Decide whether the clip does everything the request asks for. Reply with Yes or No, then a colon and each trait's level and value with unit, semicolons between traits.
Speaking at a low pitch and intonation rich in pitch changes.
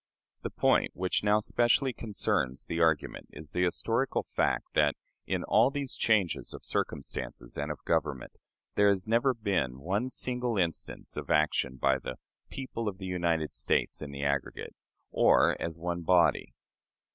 Yes: very low, 90 Hz; wide, 6.4 semitones